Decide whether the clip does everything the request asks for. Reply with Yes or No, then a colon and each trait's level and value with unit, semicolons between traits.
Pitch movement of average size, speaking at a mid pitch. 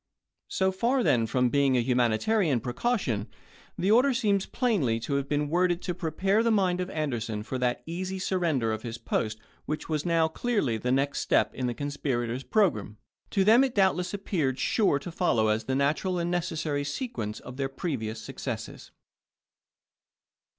No: wide, 7.3 semitones; medium, 150 Hz